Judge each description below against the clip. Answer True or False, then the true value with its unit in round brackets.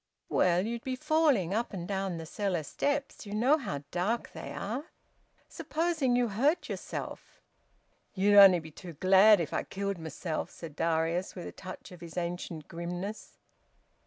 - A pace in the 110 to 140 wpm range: False (160 wpm)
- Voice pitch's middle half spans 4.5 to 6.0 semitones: True (5.6 semitones)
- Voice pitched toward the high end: True (195 Hz)